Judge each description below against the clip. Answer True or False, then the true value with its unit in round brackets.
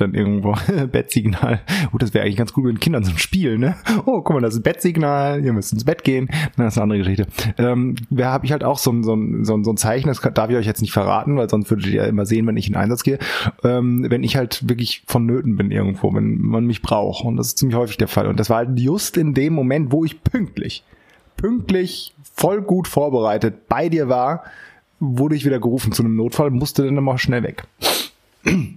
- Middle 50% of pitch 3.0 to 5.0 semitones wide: True (4.4 semitones)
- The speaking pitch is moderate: False (125 Hz)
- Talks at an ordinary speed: False (235 wpm)